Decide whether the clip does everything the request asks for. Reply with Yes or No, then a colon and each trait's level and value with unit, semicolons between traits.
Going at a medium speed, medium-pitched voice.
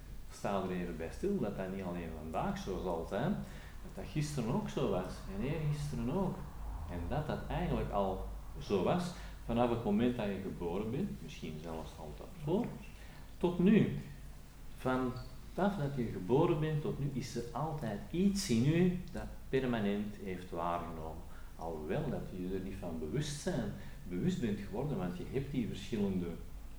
No: average, 170 wpm; low, 100 Hz